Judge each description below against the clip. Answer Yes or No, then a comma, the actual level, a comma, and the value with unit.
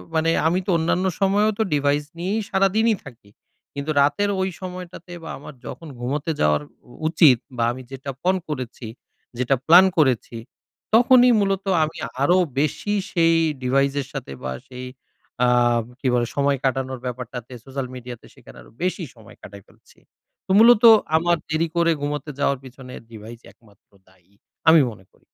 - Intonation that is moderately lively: No, wide, 5.9 semitones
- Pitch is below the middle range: No, medium, 145 Hz